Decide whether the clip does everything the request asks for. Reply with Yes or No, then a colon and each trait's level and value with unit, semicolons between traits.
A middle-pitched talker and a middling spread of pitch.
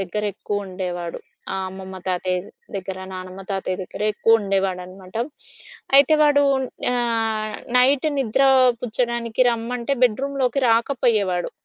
No: high, 215 Hz; average, 4.3 semitones